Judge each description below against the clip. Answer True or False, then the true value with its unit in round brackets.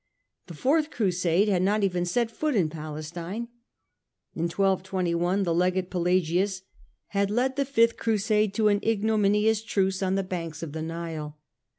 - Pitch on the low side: False (190 Hz)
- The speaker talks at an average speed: True (155 wpm)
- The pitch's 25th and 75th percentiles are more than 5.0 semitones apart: False (3.8 semitones)